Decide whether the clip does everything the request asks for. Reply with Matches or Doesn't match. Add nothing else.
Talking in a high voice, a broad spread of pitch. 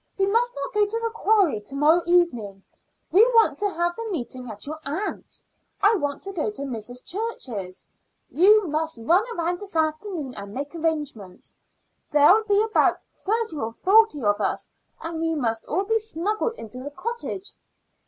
Matches